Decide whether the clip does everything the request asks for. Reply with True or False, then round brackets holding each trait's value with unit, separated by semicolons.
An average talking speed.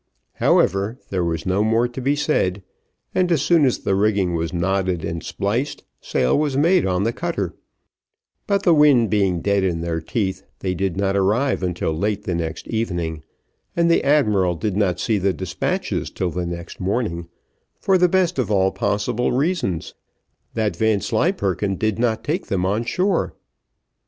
True (165 wpm)